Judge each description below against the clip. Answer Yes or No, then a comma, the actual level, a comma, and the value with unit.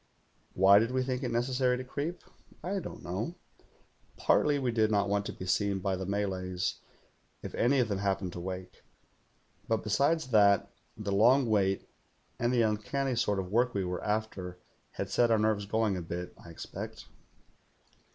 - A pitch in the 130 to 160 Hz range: No, low, 105 Hz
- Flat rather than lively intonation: No, average, 4.5 semitones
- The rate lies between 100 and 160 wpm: No, average, 180 wpm